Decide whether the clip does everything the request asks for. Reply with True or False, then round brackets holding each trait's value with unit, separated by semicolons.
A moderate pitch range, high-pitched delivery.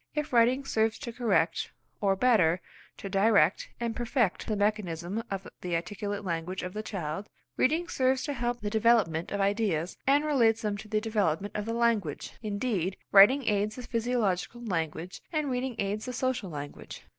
True (4.0 semitones; 215 Hz)